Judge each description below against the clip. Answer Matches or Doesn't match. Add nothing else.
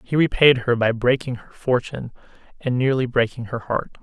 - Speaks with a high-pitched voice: Doesn't match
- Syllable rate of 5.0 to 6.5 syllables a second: Matches